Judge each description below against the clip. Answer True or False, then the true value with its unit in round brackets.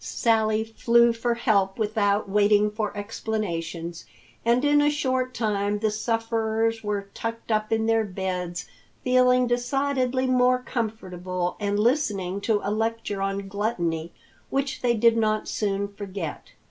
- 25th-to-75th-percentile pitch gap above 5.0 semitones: False (2.9 semitones)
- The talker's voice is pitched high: True (220 Hz)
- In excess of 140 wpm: False (135 wpm)